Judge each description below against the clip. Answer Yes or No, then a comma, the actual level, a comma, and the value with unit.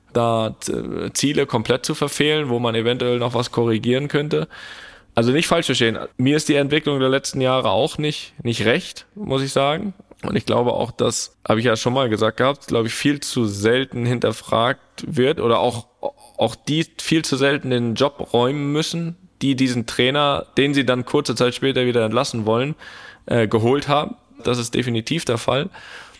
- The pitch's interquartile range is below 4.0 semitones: Yes, average, 3.6 semitones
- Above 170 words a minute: Yes, average, 185 wpm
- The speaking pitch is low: Yes, low, 130 Hz